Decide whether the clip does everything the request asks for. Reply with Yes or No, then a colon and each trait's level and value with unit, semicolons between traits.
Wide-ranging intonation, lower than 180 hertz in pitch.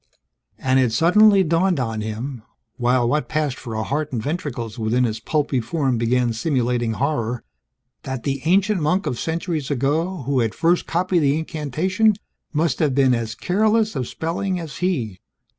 Yes: wide, 5.7 semitones; medium, 140 Hz